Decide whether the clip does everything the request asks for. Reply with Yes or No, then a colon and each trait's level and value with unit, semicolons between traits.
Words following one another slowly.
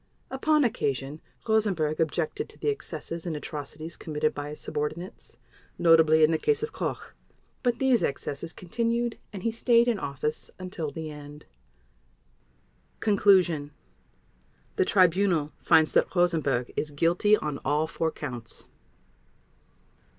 Yes: slow, 130 wpm